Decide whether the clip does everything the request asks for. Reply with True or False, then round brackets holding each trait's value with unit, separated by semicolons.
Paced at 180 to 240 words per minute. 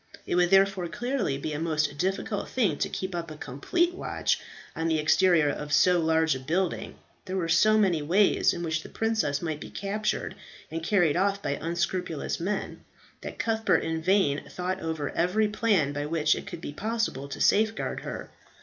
True (185 wpm)